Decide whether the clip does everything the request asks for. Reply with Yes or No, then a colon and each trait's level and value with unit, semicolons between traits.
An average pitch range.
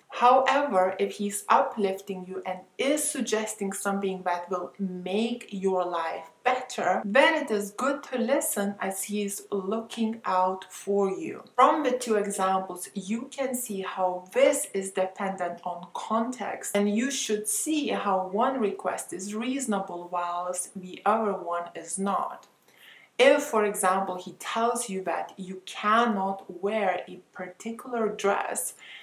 Yes: average, 3.8 semitones